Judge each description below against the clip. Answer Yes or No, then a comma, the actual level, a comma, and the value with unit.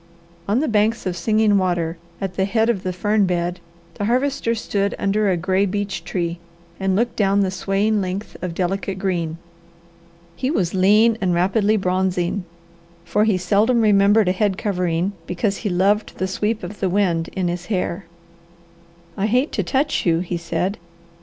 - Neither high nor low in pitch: No, high, 195 Hz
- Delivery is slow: No, average, 170 wpm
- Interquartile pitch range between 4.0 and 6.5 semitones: No, average, 2.7 semitones